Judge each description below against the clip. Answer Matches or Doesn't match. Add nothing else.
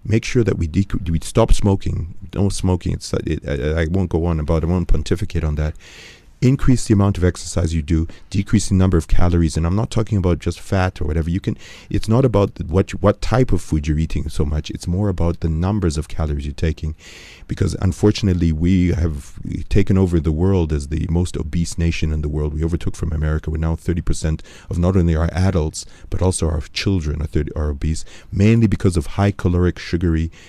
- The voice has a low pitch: Matches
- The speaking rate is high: Matches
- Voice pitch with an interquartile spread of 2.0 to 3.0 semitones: Doesn't match